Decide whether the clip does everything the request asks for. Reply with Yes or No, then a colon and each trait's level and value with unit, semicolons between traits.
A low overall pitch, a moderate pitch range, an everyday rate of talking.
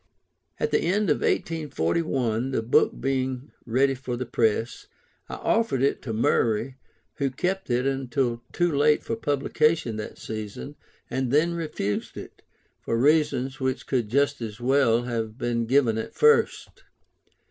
Yes: low, 130 Hz; average, 3.8 semitones; average, 145 wpm